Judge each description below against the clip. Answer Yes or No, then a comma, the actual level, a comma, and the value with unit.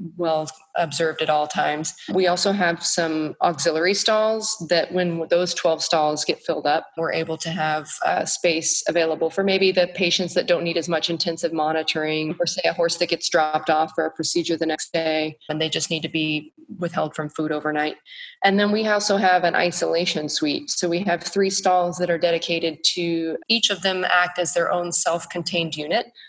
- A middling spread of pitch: No, narrow, 2.1 semitones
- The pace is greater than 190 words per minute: Yes, average, 200 wpm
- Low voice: No, medium, 170 Hz